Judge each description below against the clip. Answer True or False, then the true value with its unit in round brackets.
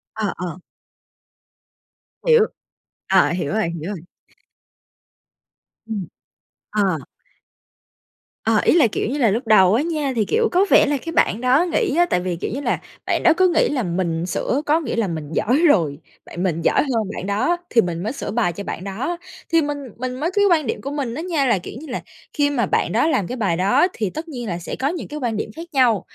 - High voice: True (235 Hz)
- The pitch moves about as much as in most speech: False (7.5 semitones)